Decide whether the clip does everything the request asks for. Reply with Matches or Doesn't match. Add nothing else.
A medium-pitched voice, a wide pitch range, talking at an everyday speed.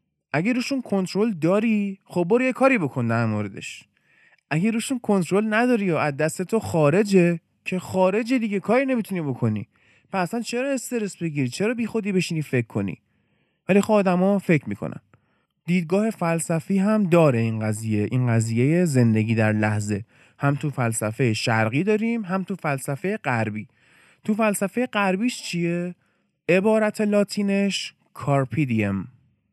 Matches